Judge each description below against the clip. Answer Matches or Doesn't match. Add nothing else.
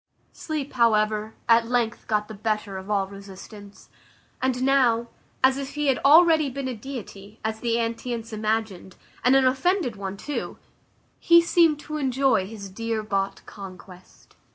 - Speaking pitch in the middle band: Doesn't match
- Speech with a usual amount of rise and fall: Matches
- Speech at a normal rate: Matches